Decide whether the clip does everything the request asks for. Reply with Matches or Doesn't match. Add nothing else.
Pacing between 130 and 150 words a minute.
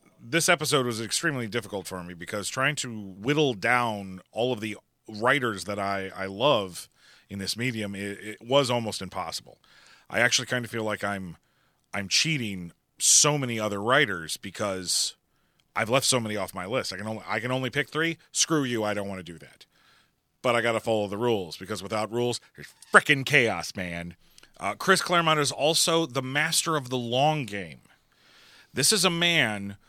Doesn't match